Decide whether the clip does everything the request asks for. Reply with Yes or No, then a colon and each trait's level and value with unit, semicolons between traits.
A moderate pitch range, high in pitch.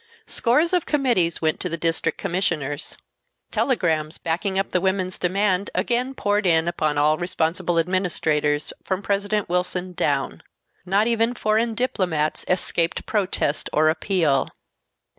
No: average, 4.0 semitones; medium, 180 Hz